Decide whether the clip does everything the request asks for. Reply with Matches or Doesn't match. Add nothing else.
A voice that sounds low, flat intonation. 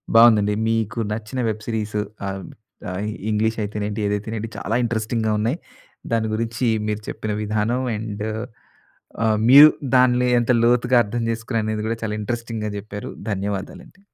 Matches